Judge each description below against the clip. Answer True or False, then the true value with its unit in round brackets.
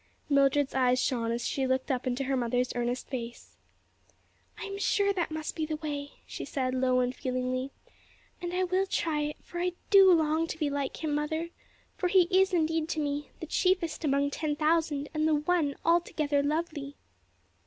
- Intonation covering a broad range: False (3.8 semitones)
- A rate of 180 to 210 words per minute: True (185 wpm)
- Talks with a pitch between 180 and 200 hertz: False (300 Hz)